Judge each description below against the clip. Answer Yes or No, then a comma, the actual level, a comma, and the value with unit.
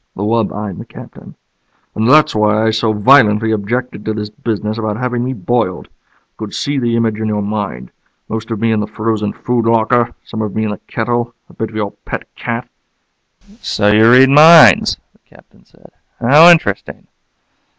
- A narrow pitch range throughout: Yes, narrow, 2.3 semitones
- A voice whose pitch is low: Yes, low, 110 Hz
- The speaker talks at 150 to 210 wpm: Yes, average, 190 wpm